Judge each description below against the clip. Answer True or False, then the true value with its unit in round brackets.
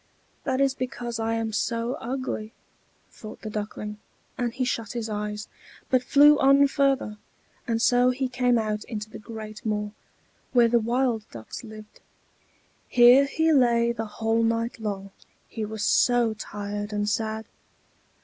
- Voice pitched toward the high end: True (230 Hz)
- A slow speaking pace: False (150 wpm)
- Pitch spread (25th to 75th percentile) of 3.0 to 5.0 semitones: False (2.6 semitones)